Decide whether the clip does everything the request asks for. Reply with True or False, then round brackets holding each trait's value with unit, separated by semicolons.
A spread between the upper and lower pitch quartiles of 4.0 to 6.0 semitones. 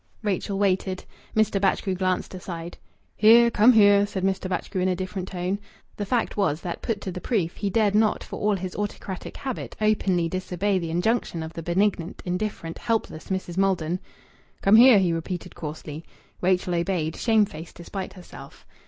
False (2.7 semitones)